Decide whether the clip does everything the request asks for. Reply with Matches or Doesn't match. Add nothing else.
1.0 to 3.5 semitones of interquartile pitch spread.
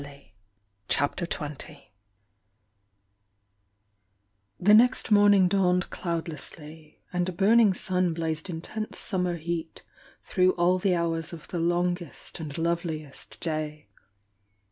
Matches